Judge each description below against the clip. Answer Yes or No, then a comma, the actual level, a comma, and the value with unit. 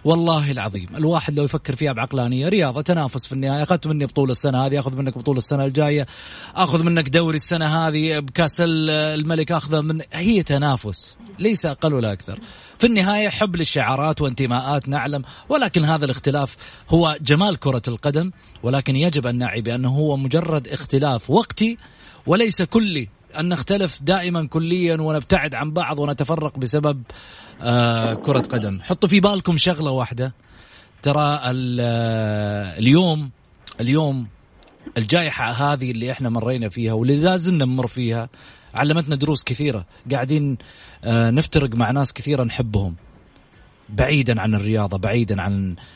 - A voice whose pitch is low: No, medium, 145 Hz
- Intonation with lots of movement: No, average, 4.6 semitones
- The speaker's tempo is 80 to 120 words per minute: No, fast, 135 wpm